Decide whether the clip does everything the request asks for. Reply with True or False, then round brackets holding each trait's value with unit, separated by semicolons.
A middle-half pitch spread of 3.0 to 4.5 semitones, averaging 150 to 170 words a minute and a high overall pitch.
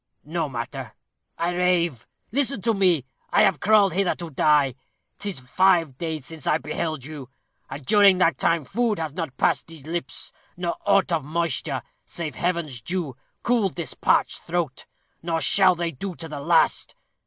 False (3.5 semitones; 165 wpm; 170 Hz)